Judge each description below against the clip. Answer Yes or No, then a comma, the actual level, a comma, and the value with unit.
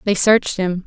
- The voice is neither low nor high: No, high, 195 Hz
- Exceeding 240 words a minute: No, fast, 210 wpm